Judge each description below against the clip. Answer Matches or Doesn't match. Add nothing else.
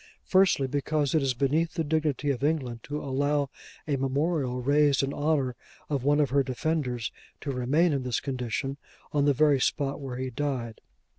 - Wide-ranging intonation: Doesn't match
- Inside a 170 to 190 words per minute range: Matches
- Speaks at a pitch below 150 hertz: Matches